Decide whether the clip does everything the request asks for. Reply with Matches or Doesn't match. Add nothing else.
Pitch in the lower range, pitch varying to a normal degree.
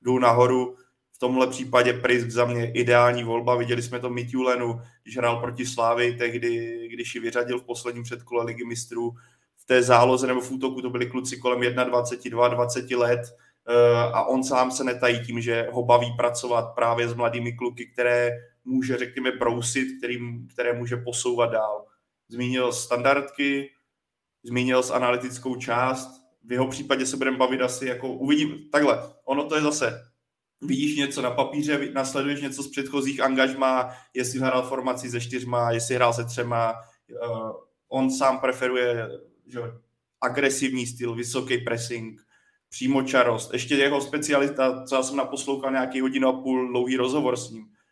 Doesn't match